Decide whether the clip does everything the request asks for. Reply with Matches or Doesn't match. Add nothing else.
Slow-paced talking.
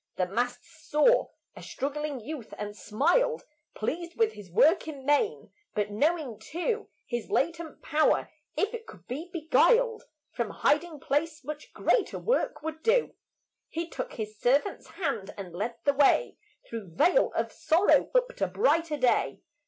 Doesn't match